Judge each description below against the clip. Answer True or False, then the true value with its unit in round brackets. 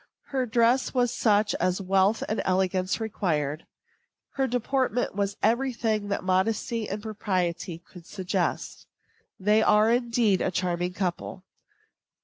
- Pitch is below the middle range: False (205 Hz)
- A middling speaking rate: False (130 wpm)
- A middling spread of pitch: True (3.8 semitones)